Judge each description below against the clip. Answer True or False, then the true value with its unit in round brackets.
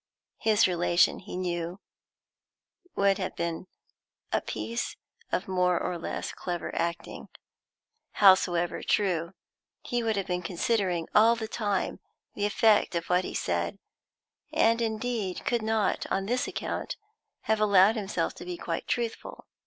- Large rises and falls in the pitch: False (3.7 semitones)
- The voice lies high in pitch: True (195 Hz)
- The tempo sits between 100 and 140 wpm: True (135 wpm)